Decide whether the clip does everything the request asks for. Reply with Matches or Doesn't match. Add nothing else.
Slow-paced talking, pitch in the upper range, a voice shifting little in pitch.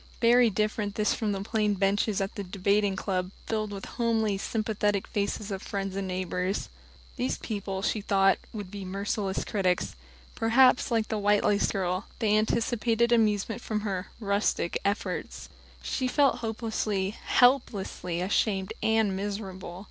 Doesn't match